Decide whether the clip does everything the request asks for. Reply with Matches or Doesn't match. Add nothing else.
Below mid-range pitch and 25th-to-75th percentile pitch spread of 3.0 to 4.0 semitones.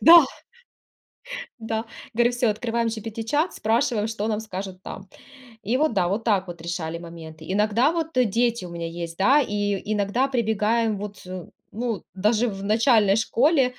Doesn't match